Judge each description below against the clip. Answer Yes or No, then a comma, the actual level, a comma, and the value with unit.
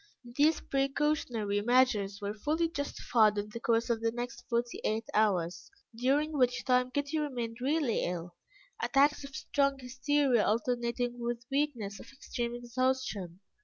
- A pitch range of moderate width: Yes, average, 3.8 semitones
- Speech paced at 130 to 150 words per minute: Yes, average, 140 wpm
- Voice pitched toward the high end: Yes, high, 245 Hz